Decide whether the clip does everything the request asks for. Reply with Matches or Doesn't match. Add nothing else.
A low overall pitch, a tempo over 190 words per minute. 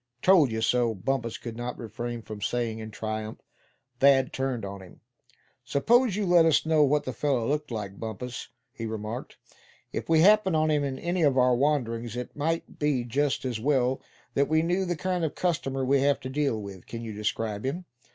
Matches